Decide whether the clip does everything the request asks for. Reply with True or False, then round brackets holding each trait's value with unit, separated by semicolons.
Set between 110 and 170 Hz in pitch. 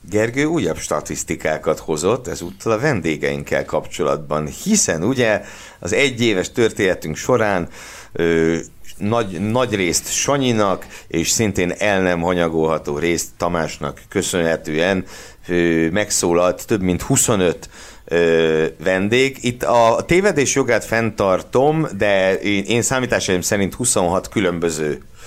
False (95 Hz)